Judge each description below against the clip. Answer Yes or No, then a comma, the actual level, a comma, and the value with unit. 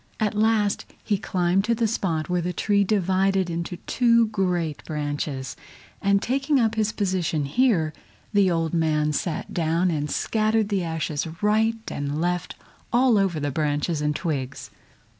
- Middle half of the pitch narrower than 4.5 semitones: No, average, 5.2 semitones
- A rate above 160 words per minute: No, average, 155 wpm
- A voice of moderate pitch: Yes, medium, 180 Hz